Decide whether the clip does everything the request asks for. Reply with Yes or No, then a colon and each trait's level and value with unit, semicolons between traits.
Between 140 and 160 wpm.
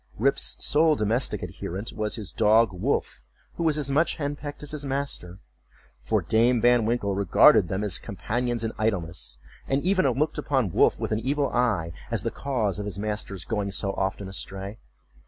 No: average, 180 wpm